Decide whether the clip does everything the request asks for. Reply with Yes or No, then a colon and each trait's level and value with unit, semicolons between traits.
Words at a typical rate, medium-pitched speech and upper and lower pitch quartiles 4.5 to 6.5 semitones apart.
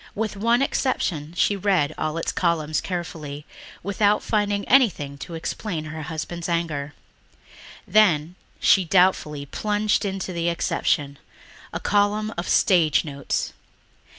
No: slow, 125 wpm; medium, 175 Hz; average, 4.8 semitones